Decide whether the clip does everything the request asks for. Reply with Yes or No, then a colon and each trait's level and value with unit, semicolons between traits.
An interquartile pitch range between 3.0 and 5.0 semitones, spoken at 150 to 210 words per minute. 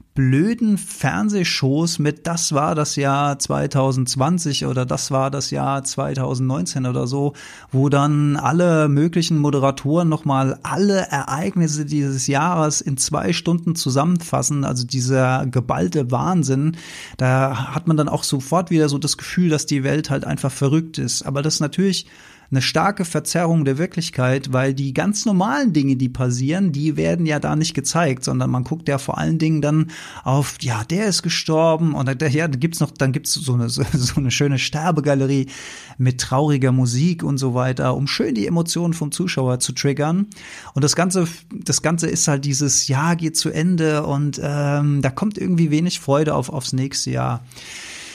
Yes: average, 3.4 semitones; average, 170 wpm